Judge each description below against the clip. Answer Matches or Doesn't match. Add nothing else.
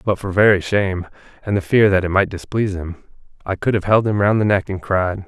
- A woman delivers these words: Doesn't match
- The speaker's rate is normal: Doesn't match